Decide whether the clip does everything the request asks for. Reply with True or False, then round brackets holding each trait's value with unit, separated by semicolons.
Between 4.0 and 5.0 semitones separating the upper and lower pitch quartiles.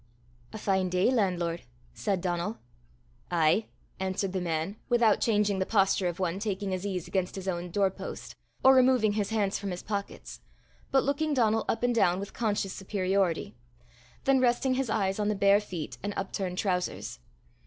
False (2.9 semitones)